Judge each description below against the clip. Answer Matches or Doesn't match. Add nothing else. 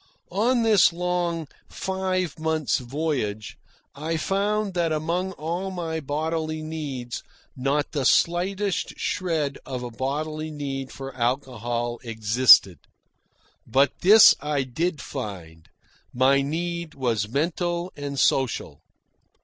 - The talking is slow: Matches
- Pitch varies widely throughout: Doesn't match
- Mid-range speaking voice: Matches